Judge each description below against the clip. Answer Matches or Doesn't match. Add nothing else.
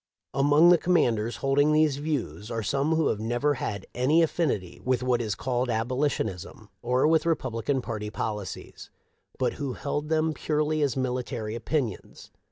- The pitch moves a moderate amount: Matches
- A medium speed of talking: Matches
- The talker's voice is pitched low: Matches